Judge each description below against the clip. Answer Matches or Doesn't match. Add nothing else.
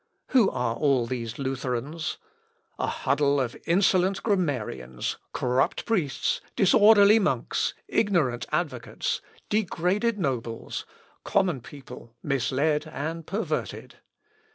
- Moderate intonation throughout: Doesn't match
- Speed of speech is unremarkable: Doesn't match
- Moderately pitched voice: Matches